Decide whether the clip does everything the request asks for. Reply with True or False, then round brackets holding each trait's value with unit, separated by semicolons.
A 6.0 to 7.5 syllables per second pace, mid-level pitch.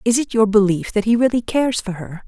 False (6.1 syllables/s; 215 Hz)